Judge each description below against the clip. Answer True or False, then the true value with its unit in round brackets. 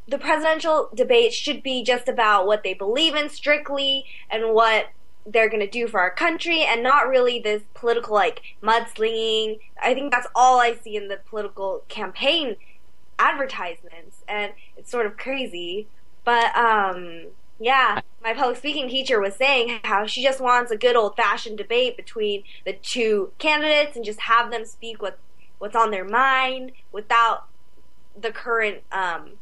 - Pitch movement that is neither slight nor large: True (4.2 semitones)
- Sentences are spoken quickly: False (165 wpm)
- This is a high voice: True (235 Hz)